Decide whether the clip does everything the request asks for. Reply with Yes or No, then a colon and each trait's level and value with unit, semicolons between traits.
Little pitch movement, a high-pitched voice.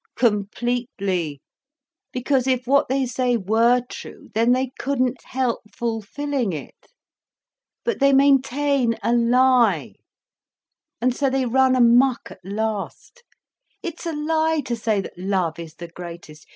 No: average, 3.9 semitones; high, 245 Hz